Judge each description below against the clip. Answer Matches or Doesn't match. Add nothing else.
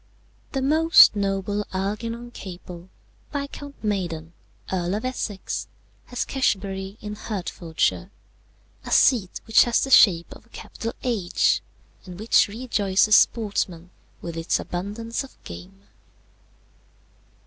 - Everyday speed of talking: Doesn't match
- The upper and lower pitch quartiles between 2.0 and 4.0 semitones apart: Doesn't match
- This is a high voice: Matches